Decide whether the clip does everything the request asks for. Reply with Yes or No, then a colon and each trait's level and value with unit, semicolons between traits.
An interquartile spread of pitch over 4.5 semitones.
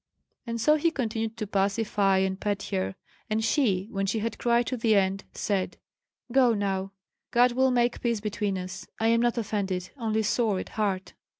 No: average, 3.2 semitones